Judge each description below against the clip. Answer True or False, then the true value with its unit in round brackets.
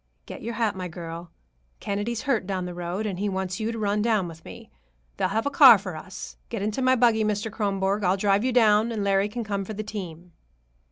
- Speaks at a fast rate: True (230 wpm)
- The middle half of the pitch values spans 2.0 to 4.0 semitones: True (3.0 semitones)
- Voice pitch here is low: False (205 Hz)